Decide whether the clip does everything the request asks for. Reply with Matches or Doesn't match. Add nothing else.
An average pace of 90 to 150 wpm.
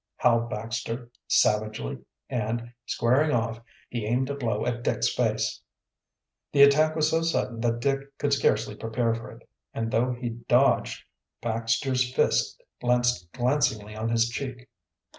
Matches